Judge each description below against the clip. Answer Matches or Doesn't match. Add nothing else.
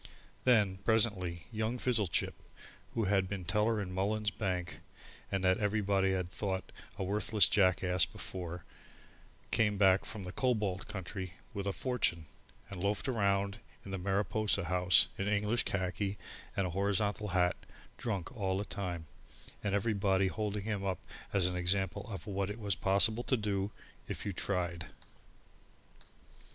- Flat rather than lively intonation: Matches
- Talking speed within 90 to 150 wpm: Matches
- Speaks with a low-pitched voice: Matches